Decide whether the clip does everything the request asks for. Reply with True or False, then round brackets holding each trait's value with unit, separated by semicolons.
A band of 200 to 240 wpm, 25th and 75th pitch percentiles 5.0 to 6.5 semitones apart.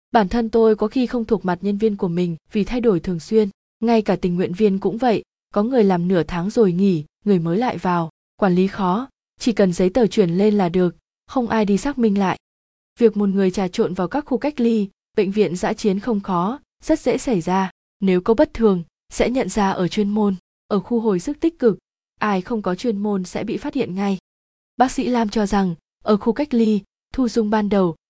False (235 wpm; 3.7 semitones)